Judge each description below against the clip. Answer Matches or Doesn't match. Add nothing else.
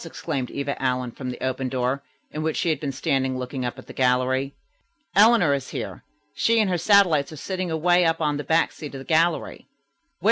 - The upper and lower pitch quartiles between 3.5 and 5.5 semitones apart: Matches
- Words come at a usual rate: Doesn't match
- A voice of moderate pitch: Matches